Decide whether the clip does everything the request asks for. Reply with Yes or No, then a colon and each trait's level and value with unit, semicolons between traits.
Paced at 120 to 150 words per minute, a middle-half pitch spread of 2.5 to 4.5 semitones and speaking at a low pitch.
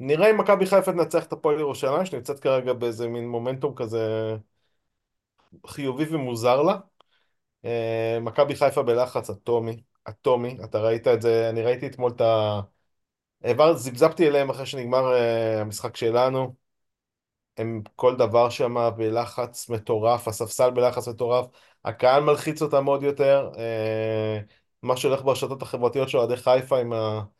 Yes: average, 130 wpm; average, 3.2 semitones; low, 120 Hz